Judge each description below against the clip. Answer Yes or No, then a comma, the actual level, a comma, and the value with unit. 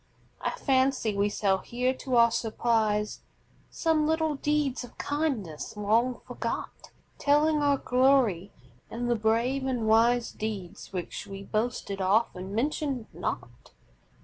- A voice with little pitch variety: No, average, 4.5 semitones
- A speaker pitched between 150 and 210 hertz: No, high, 235 Hz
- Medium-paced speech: No, slow, 125 wpm